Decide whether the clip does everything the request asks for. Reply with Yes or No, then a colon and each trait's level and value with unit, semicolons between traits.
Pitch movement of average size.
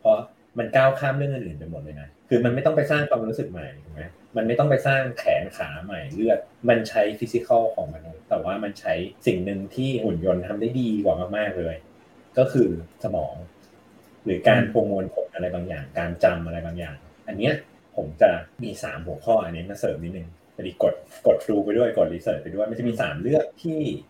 No: wide, 7.7 semitones